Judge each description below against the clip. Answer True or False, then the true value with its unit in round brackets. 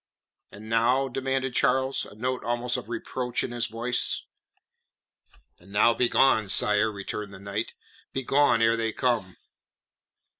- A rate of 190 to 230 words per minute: False (135 wpm)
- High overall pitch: False (115 Hz)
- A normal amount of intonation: True (3.0 semitones)